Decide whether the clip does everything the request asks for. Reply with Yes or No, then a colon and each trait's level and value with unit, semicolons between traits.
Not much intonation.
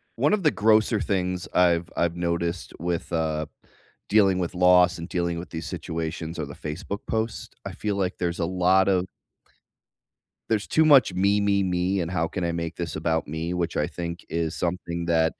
Yes: narrow, 2.2 semitones